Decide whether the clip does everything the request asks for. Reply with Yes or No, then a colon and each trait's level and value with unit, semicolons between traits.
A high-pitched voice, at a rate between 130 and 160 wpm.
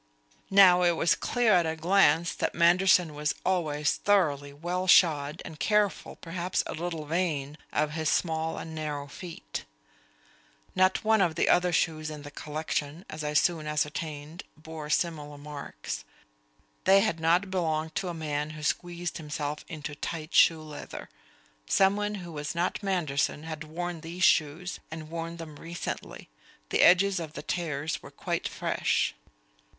No: medium, 160 Hz; average, 155 wpm